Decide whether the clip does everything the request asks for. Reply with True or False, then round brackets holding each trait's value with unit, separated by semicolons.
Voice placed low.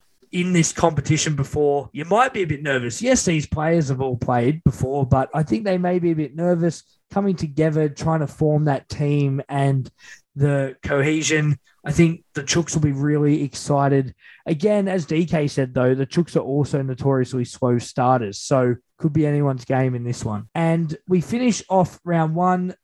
False (150 Hz)